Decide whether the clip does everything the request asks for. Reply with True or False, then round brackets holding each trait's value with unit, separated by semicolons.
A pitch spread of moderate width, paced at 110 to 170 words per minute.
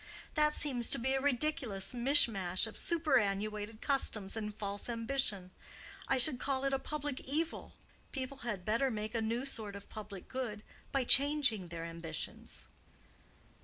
True (4.8 semitones; 150 wpm)